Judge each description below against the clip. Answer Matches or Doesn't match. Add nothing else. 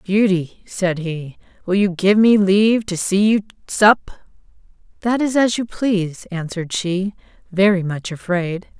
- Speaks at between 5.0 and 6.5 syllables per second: Doesn't match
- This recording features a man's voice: Doesn't match